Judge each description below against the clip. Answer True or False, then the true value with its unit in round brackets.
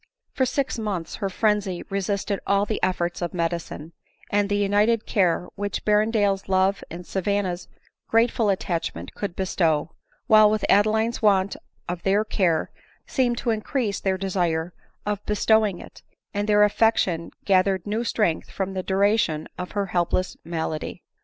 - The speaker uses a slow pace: False (150 wpm)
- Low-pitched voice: False (195 Hz)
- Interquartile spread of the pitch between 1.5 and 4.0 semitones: True (2.8 semitones)